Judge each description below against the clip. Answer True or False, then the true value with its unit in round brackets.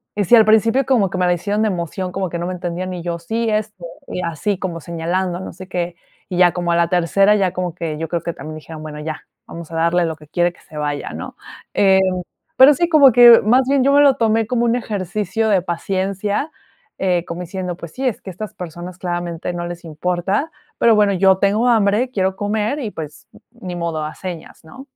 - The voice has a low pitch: False (185 Hz)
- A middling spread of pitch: True (3.9 semitones)